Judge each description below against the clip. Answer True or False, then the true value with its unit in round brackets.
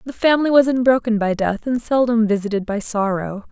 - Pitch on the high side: True (225 Hz)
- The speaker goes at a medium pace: True (190 wpm)